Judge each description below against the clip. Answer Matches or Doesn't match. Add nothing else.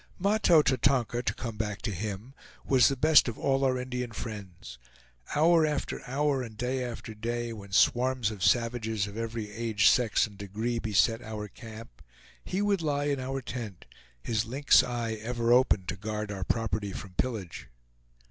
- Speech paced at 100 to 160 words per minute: Doesn't match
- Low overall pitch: Matches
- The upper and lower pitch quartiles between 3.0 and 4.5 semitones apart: Matches